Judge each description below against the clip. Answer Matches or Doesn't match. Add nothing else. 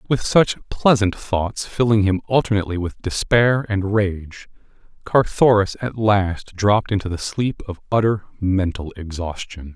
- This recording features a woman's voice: Doesn't match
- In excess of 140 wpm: Doesn't match